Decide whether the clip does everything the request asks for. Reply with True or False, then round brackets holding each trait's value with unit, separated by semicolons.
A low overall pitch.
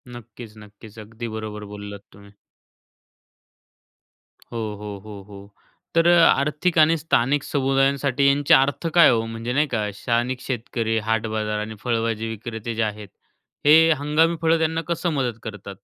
True (120 Hz)